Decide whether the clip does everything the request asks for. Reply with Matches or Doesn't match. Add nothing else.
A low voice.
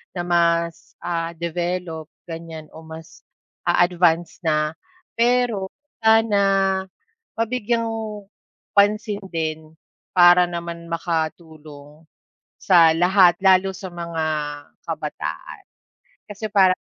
Doesn't match